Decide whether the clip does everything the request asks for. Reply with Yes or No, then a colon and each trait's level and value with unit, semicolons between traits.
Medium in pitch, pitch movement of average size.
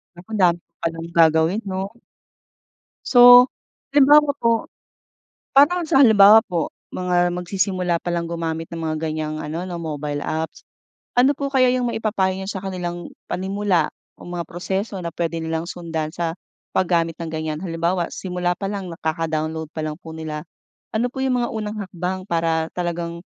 Yes: medium, 175 Hz; average, 3.4 semitones